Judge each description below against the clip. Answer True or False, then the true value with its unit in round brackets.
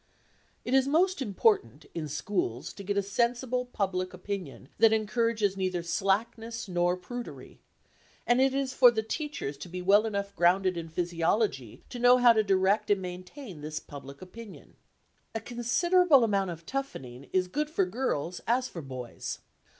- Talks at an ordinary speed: True (160 wpm)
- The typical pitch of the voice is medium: False (200 Hz)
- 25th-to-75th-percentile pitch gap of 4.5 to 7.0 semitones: True (5.3 semitones)